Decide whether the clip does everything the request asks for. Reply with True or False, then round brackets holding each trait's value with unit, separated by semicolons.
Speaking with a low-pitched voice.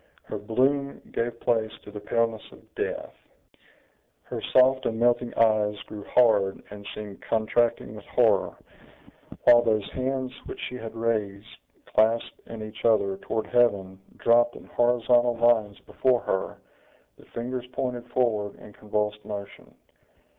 True (115 Hz)